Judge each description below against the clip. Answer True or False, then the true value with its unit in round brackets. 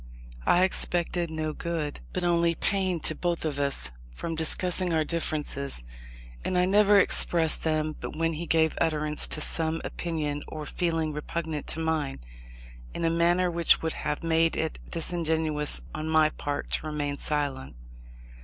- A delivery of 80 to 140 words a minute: False (155 wpm)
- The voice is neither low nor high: True (160 Hz)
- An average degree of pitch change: False (1.9 semitones)